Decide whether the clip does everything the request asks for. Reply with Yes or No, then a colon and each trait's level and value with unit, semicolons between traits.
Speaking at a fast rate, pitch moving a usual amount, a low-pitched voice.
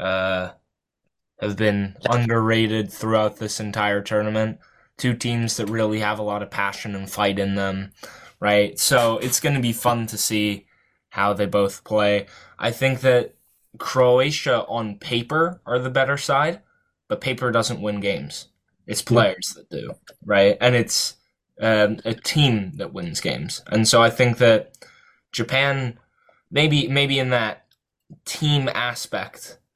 No: average, 145 wpm; average, 3.7 semitones; low, 115 Hz